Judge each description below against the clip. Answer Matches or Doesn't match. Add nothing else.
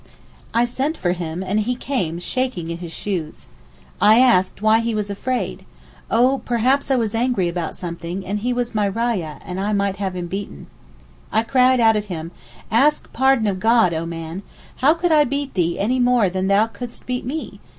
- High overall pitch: Matches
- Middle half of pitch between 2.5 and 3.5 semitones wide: Doesn't match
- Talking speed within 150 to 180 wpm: Doesn't match